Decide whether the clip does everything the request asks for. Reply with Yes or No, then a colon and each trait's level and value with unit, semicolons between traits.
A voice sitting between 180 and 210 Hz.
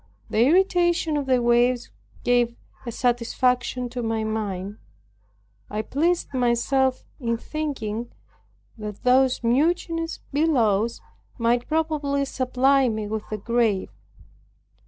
No: high, 245 Hz